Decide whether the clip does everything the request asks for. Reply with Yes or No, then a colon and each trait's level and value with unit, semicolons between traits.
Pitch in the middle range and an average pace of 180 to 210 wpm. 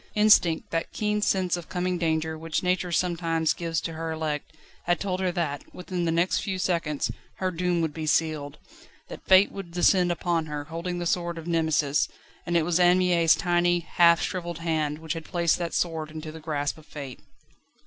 Yes: medium, 170 Hz; average, 195 wpm